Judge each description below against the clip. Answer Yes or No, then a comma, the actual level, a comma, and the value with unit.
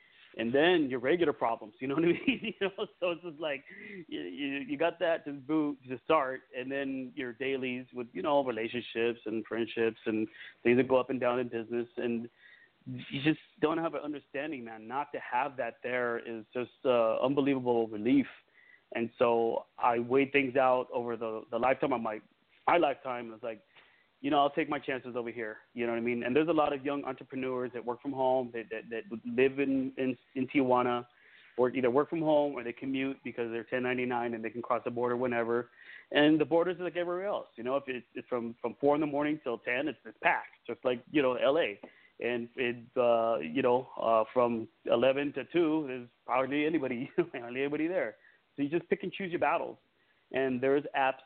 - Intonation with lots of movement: No, average, 3.5 semitones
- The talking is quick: Yes, fast, 215 wpm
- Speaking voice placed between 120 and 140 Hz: Yes, low, 130 Hz